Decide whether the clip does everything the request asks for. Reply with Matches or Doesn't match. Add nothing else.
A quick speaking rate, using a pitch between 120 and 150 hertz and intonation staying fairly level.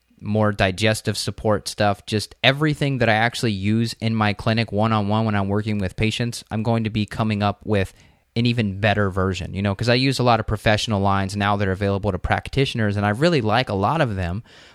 Doesn't match